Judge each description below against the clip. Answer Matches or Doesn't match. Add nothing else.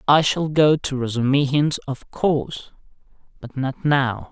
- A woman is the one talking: Doesn't match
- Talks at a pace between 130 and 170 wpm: Matches